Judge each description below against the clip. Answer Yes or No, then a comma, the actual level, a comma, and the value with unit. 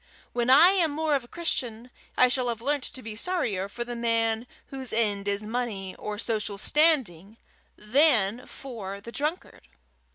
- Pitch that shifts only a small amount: No, average, 4.4 semitones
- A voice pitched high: Yes, high, 235 Hz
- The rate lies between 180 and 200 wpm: No, average, 165 wpm